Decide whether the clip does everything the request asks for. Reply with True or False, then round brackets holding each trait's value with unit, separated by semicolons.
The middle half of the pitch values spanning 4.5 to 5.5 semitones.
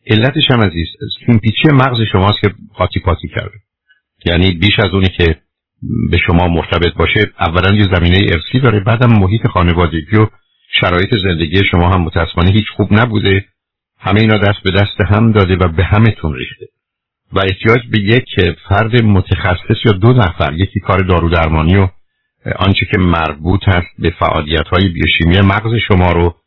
False (3.6 semitones)